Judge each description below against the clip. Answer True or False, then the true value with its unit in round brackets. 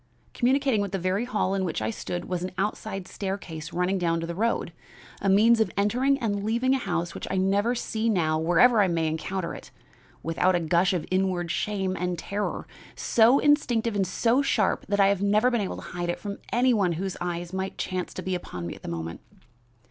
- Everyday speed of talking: False (215 wpm)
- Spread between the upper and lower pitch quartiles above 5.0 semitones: False (3.9 semitones)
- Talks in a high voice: True (195 Hz)